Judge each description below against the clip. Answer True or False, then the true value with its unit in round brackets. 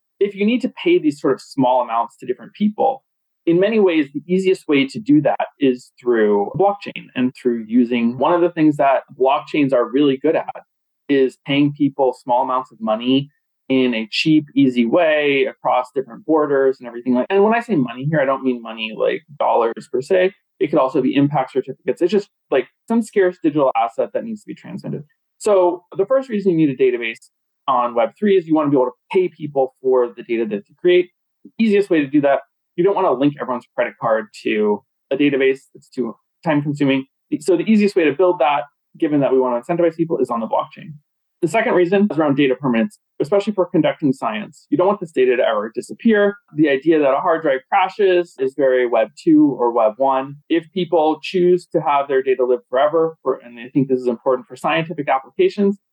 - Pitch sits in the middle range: True (155 Hz)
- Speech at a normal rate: False (215 wpm)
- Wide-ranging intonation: True (6.8 semitones)